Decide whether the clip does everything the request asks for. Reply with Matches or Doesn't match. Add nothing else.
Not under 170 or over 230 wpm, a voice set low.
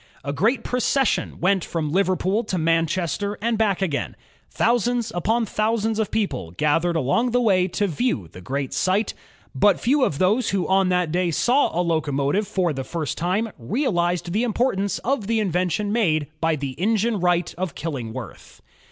Doesn't match